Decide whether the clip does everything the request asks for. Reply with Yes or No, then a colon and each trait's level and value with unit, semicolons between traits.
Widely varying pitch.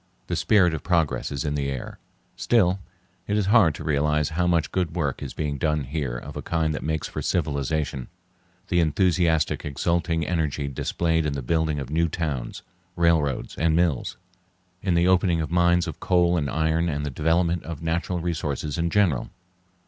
No: average, 2.9 semitones